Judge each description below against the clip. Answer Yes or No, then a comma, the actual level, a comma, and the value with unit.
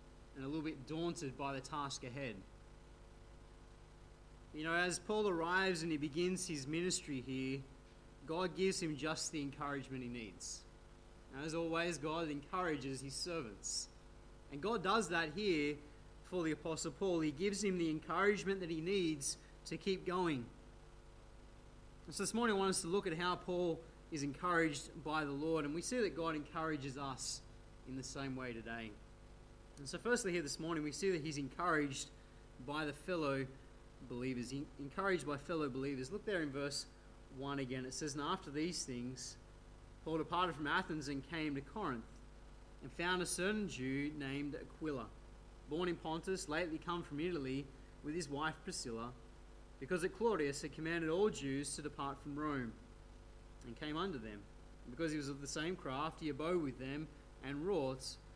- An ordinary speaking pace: Yes, average, 175 wpm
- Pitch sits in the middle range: Yes, medium, 150 Hz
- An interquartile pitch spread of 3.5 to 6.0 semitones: Yes, average, 4.1 semitones